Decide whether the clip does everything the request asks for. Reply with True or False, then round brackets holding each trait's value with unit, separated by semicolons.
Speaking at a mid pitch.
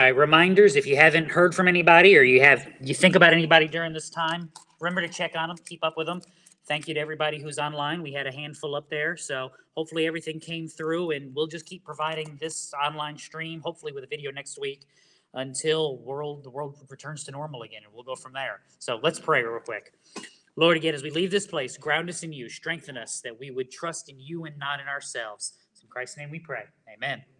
True (155 Hz)